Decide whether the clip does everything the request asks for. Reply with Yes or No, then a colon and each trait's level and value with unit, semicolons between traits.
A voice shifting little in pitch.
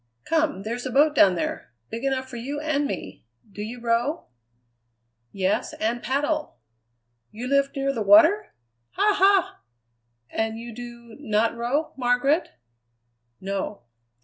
No: average, 4.4 semitones